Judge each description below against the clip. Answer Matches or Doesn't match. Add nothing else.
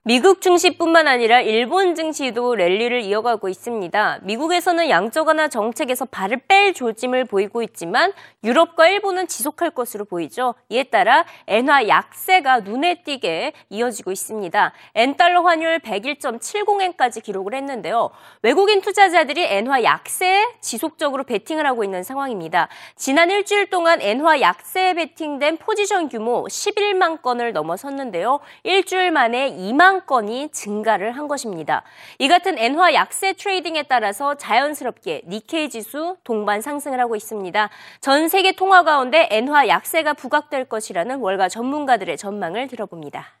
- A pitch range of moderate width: Doesn't match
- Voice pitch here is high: Matches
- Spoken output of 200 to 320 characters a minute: Doesn't match